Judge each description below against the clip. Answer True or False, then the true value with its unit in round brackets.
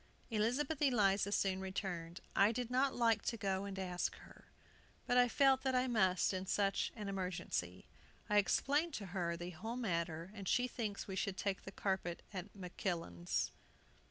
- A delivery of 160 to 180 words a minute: True (170 wpm)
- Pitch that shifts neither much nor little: True (4.3 semitones)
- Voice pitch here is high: True (195 Hz)